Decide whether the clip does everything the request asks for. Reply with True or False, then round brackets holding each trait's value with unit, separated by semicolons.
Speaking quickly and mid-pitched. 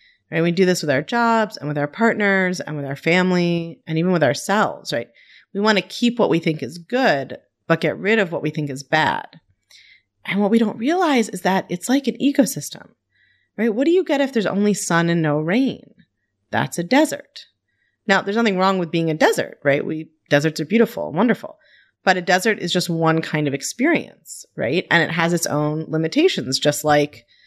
True (215 wpm; 180 Hz)